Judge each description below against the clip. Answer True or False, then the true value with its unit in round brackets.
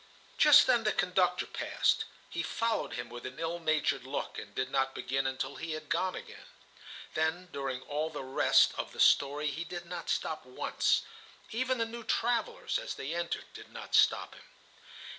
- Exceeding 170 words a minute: True (180 wpm)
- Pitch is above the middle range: False (160 Hz)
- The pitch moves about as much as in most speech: False (7.7 semitones)